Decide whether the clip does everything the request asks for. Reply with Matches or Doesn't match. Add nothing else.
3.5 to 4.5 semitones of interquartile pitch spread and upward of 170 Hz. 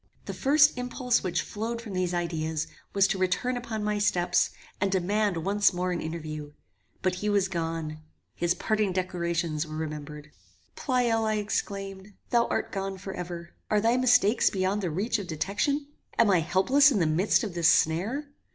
Matches